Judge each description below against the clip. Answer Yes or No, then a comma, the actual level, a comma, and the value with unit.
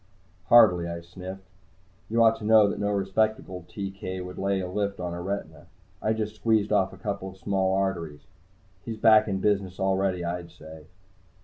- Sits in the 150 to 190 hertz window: No, very low, 95 Hz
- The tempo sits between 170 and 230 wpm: Yes, average, 180 wpm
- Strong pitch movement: No, narrow, 2.5 semitones